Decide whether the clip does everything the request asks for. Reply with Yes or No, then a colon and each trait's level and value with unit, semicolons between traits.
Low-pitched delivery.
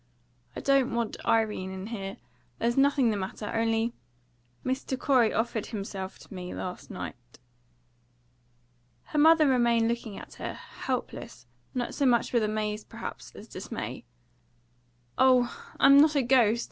No: high, 235 Hz